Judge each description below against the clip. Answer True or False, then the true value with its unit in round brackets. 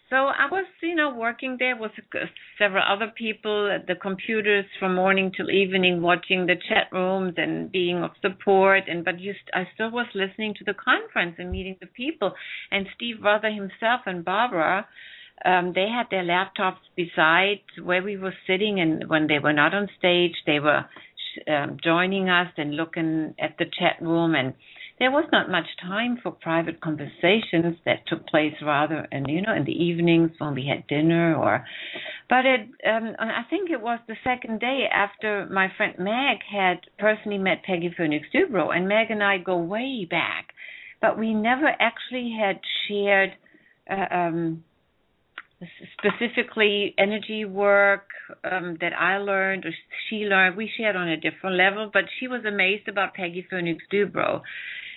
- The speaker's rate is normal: True (170 wpm)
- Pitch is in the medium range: False (195 Hz)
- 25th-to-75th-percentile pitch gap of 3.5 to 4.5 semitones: True (3.8 semitones)